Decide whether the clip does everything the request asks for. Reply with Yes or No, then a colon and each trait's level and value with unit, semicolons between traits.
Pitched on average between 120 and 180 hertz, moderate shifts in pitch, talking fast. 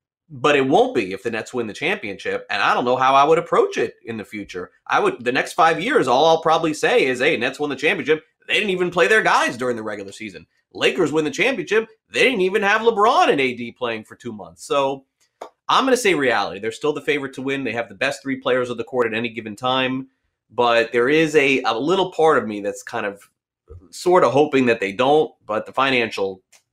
No: low, 135 Hz; wide, 5.7 semitones; fast, 245 wpm